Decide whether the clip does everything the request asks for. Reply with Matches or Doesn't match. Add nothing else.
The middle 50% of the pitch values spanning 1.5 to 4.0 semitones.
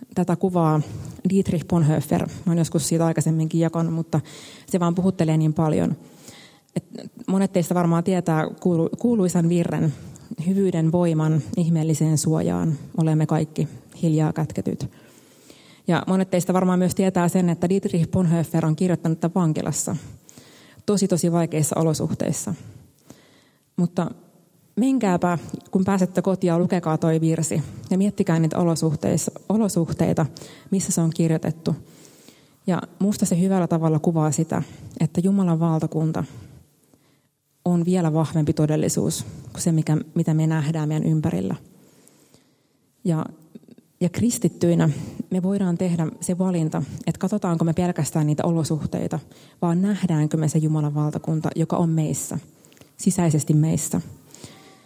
Matches